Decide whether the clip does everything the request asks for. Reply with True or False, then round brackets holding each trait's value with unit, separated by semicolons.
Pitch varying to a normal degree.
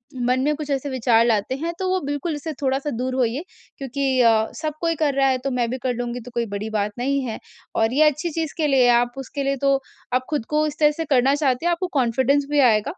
True (3.3 semitones)